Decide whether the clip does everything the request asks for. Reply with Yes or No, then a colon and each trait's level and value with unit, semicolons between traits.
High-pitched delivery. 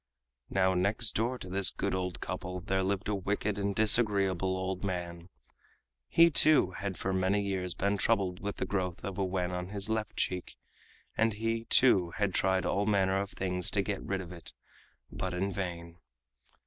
No: very low, 95 Hz